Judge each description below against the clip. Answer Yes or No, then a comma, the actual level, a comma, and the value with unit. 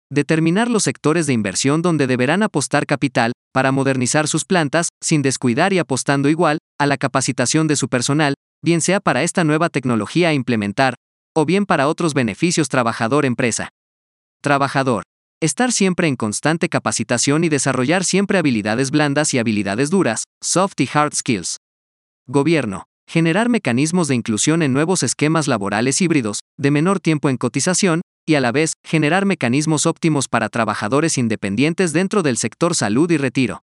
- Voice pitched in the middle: Yes, medium, 145 Hz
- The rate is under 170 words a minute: Yes, average, 155 wpm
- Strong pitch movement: No, average, 4.6 semitones